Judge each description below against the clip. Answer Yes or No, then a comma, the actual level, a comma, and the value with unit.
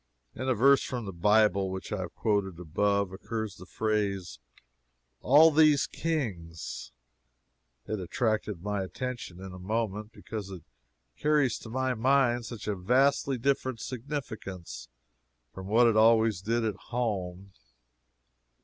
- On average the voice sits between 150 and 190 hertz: No, low, 110 Hz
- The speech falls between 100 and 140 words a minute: Yes, slow, 135 wpm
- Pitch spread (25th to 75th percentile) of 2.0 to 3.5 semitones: No, average, 4.6 semitones